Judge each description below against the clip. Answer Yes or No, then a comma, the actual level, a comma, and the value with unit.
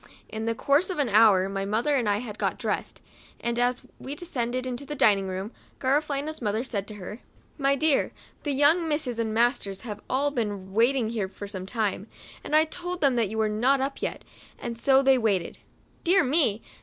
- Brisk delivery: Yes, fast, 210 wpm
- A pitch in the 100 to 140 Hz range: No, high, 240 Hz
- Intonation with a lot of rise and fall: No, average, 4.9 semitones